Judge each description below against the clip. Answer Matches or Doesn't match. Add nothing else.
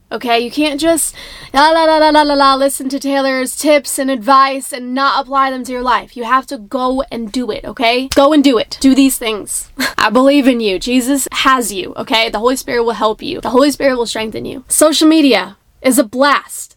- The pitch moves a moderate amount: Doesn't match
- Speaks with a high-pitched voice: Matches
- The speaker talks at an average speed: Doesn't match